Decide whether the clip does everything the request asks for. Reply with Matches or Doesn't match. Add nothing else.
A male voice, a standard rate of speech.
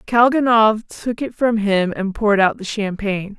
Doesn't match